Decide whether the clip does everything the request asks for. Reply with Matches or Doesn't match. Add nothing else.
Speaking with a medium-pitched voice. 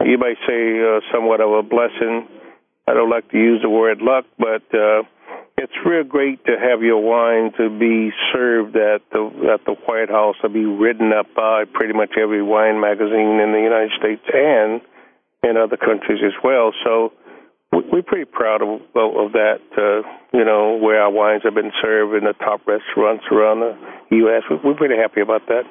Doesn't match